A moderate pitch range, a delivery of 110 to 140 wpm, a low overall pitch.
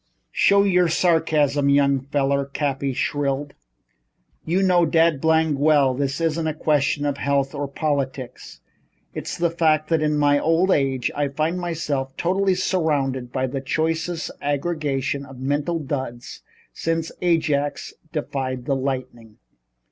No: average, 3.1 semitones; slow, 135 wpm; medium, 145 Hz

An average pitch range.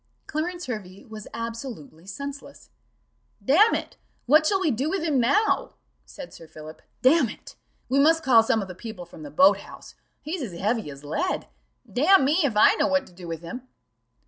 No: wide, 7.4 semitones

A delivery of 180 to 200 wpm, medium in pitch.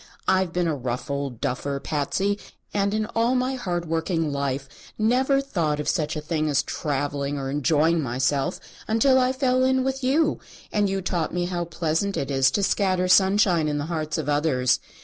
Yes: average, 190 wpm; medium, 165 Hz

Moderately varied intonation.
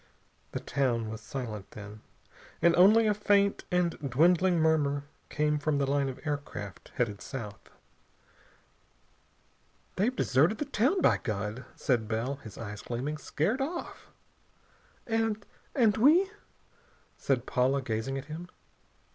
No: wide, 8.5 semitones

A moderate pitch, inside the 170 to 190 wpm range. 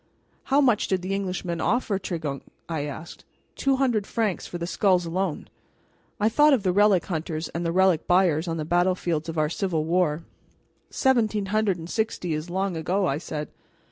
Yes: medium, 180 Hz; average, 180 wpm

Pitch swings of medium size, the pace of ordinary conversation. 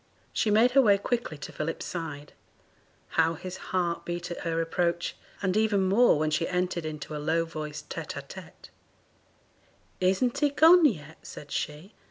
Yes: average, 4.7 semitones; average, 170 wpm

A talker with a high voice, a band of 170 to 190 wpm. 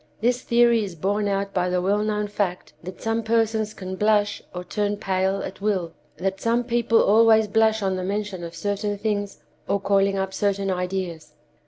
Yes: high, 200 Hz; average, 185 wpm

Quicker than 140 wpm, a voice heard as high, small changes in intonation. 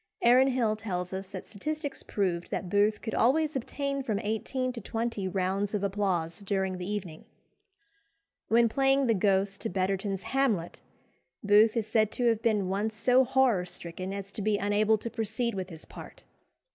No: average, 170 wpm; high, 210 Hz; average, 3.5 semitones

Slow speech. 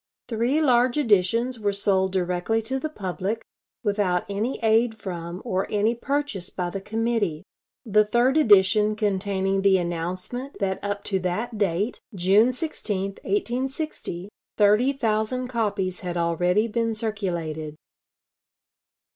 Yes: slow, 125 wpm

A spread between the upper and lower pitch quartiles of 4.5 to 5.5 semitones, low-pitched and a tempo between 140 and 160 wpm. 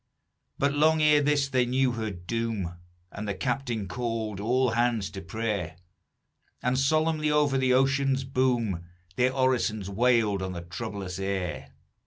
Yes: average, 5.0 semitones; low, 120 Hz; average, 145 wpm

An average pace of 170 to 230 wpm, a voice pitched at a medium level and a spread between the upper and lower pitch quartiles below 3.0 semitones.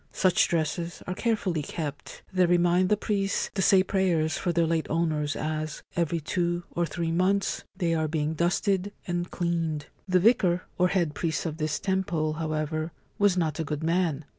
Yes: average, 175 wpm; medium, 170 Hz; narrow, 2.6 semitones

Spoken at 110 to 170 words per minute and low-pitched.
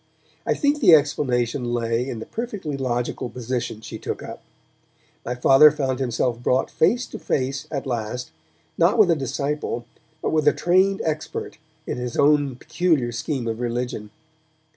Yes: average, 160 wpm; low, 130 Hz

